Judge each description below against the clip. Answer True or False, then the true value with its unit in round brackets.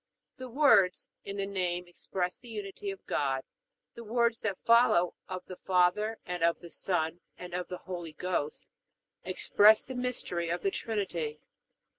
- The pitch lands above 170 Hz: True (185 Hz)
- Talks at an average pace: True (160 wpm)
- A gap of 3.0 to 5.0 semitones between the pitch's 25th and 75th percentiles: True (3.6 semitones)